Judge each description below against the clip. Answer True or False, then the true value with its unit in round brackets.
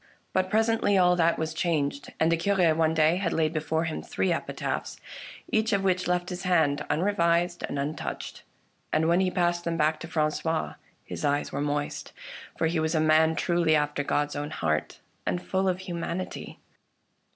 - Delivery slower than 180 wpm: False (185 wpm)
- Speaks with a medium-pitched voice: True (165 Hz)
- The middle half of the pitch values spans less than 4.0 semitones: True (2.4 semitones)